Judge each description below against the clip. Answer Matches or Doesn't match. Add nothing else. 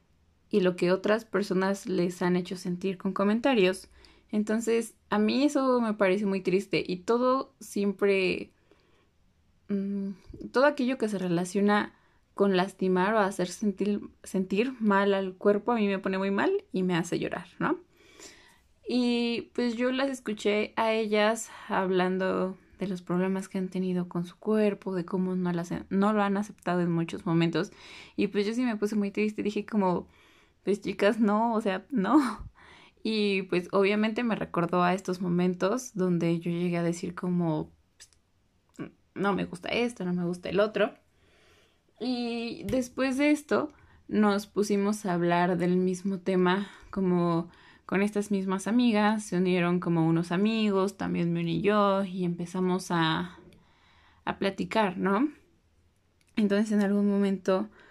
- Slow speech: Doesn't match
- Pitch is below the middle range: Doesn't match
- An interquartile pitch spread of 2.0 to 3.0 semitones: Matches